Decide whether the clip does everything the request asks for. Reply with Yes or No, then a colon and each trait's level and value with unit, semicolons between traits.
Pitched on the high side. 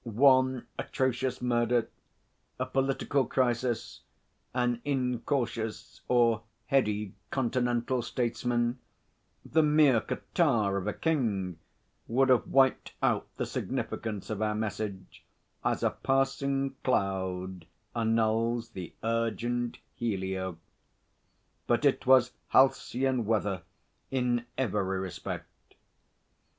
No: low, 120 Hz